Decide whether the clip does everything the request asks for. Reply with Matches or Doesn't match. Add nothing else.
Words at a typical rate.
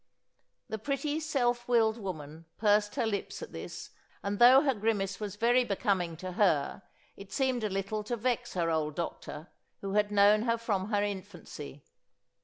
Matches